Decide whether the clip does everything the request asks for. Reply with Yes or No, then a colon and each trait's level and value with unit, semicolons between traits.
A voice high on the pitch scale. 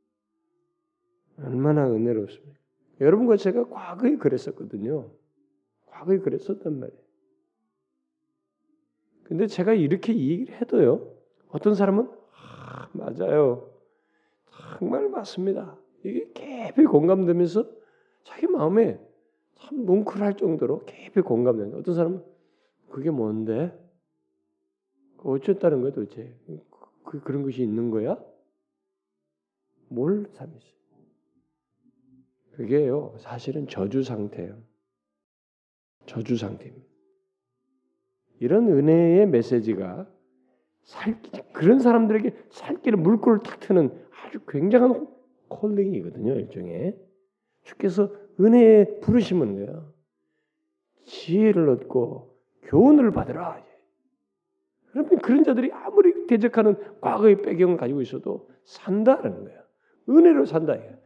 Yes: high, 195 Hz